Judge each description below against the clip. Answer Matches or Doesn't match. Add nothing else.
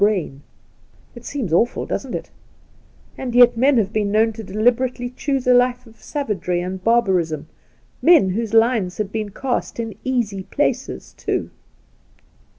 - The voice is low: Doesn't match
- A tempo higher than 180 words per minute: Doesn't match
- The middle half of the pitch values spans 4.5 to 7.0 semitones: Doesn't match